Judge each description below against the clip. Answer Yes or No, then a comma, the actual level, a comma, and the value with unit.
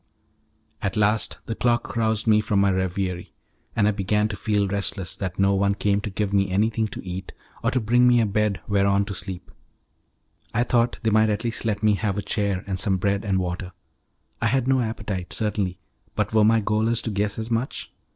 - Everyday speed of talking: No, fast, 210 wpm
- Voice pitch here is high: No, low, 105 Hz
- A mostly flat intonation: Yes, narrow, 2.1 semitones